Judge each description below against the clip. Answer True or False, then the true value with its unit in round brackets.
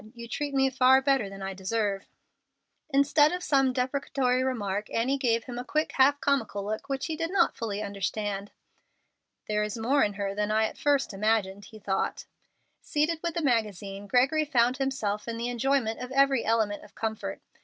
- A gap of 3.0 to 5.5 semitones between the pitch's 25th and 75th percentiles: True (4.7 semitones)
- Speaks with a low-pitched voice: False (240 Hz)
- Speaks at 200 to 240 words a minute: False (185 wpm)